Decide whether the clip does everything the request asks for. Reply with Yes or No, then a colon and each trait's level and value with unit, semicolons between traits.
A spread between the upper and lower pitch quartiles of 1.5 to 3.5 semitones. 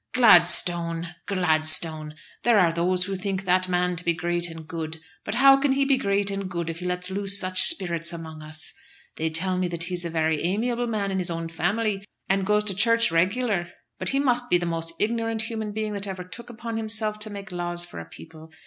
No: average, 4.0 semitones